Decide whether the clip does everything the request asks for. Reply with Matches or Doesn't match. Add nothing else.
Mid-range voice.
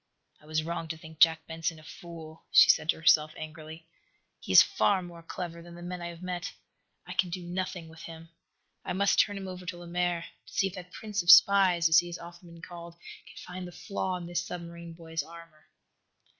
Matches